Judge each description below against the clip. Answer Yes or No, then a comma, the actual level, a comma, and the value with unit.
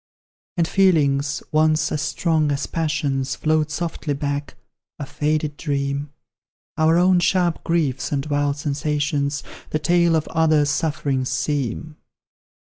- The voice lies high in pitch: No, medium, 150 Hz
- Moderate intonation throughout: No, narrow, 2.0 semitones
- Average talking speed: No, slow, 125 wpm